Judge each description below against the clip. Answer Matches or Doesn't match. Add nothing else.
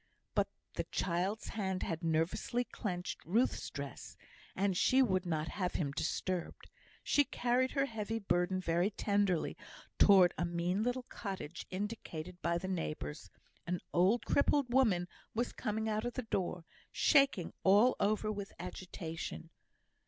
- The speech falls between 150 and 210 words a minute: Doesn't match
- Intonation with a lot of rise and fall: Doesn't match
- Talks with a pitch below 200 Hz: Matches